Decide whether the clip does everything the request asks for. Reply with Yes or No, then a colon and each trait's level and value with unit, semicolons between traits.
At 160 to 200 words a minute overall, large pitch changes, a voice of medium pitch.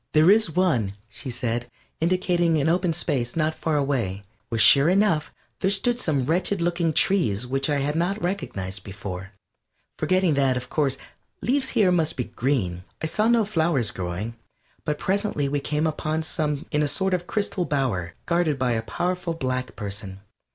Yes: average, 170 wpm; wide, 6.2 semitones; medium, 150 Hz